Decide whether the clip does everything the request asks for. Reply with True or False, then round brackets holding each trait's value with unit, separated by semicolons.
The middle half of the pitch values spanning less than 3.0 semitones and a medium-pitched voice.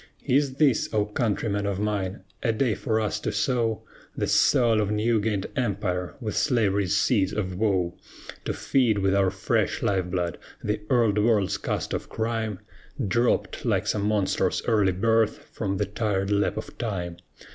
False (2.6 semitones; 105 Hz)